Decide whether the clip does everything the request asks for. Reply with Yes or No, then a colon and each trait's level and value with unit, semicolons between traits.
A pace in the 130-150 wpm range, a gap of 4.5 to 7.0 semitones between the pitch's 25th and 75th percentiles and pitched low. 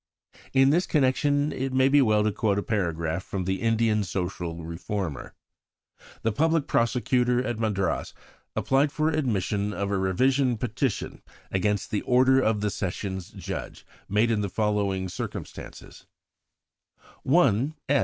Yes: average, 140 wpm; average, 5.1 semitones; low, 110 Hz